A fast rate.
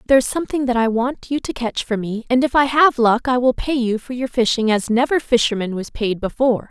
Yes: fast, 260 wpm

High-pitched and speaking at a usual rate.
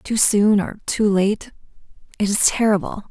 Yes: high, 205 Hz; average, 155 wpm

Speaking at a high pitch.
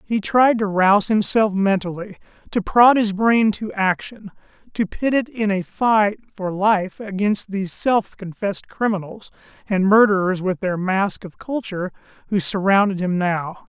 Yes: high, 200 Hz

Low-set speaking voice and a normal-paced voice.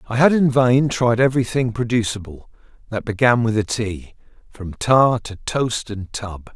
Yes: low, 115 Hz; average, 165 wpm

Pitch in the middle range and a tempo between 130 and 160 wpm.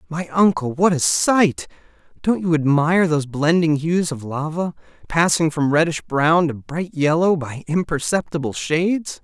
Yes: medium, 160 Hz; average, 150 wpm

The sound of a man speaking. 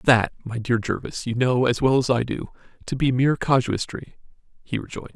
Yes: male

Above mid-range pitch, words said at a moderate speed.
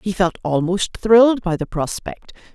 Yes: high, 195 Hz; average, 165 wpm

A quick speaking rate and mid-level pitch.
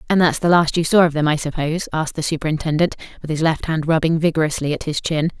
Yes: fast, 245 wpm; medium, 160 Hz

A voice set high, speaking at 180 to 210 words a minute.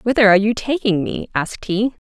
Yes: high, 215 Hz; fast, 205 wpm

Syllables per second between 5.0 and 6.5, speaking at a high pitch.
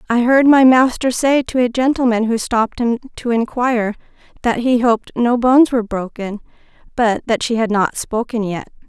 Yes: 5.2 syllables/s; high, 235 Hz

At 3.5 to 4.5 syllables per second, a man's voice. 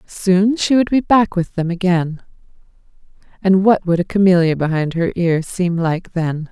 No: 4.4 syllables/s; female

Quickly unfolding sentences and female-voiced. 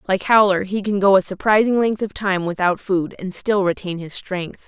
Yes: fast, 220 wpm; female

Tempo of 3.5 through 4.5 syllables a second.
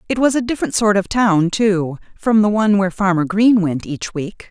No: 5.3 syllables/s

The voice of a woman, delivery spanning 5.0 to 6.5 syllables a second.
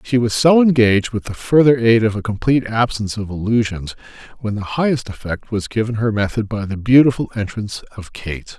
No: male; 5.7 syllables/s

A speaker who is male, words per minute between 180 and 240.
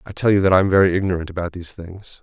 No: male; fast, 295 wpm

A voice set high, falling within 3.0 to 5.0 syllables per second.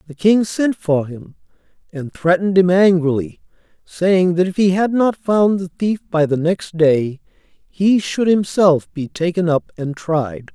No: medium, 175 Hz; 4.1 syllables/s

